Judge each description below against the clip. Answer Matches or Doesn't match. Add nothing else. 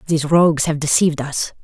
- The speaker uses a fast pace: Doesn't match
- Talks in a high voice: Doesn't match